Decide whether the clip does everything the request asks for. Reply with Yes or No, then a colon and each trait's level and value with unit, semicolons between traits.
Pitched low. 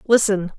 No: high, 200 Hz